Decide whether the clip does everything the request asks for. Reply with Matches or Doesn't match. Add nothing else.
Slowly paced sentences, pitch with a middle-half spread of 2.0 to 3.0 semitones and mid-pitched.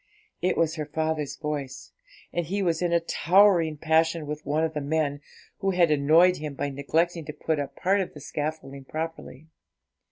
Doesn't match